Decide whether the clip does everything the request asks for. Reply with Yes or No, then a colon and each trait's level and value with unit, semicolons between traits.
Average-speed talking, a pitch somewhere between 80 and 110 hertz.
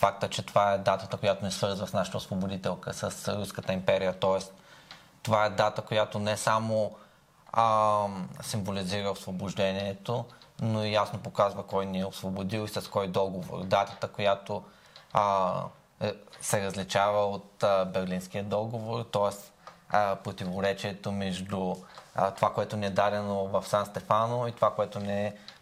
Yes: average, 145 wpm; low, 100 Hz